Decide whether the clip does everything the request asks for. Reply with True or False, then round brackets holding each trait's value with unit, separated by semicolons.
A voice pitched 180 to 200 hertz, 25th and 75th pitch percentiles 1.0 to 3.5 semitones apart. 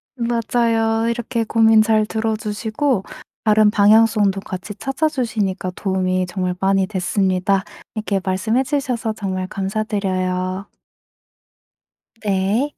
False (210 Hz; 3.0 semitones)